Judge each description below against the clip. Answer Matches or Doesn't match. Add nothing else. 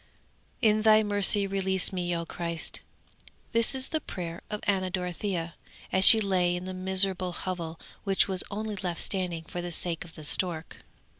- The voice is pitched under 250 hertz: Matches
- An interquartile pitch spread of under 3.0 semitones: Matches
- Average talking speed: Matches